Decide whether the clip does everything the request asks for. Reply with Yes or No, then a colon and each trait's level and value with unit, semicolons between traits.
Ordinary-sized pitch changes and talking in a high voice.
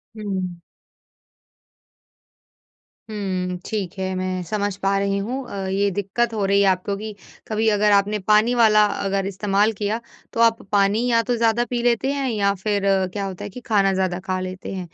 No: narrow, 2.2 semitones; high, 200 Hz